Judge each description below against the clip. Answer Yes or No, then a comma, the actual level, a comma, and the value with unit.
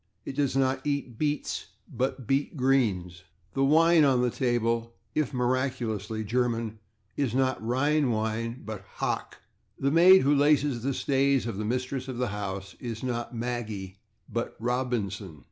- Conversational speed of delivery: Yes, average, 150 wpm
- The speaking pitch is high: No, low, 125 Hz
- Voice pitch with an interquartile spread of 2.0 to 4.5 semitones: Yes, average, 3.5 semitones